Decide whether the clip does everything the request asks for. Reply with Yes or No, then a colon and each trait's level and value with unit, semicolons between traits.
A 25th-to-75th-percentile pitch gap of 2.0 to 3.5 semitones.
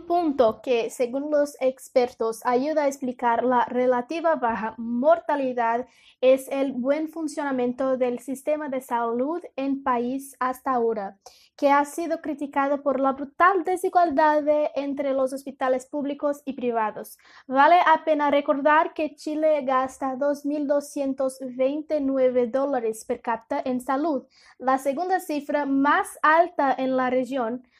Yes: average, 2.9 semitones